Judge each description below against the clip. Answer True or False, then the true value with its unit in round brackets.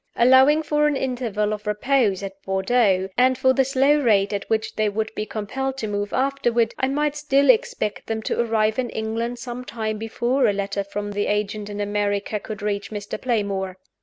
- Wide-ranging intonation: False (4.1 semitones)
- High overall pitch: True (220 Hz)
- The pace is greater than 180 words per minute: True (190 wpm)